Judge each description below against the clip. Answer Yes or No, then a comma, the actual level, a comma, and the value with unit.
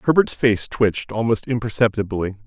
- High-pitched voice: No, low, 110 Hz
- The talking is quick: No, slow, 120 wpm